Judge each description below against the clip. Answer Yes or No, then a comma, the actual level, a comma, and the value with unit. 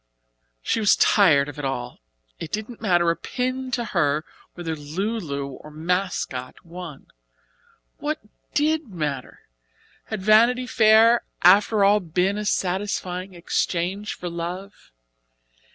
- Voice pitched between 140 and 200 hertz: Yes, medium, 185 Hz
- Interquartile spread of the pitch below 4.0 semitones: No, average, 4.9 semitones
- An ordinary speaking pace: No, slow, 125 wpm